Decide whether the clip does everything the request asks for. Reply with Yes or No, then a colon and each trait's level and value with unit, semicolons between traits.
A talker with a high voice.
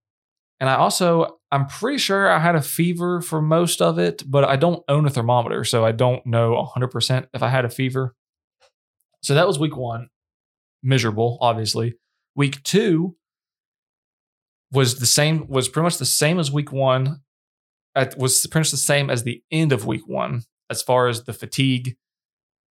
No: low, 130 Hz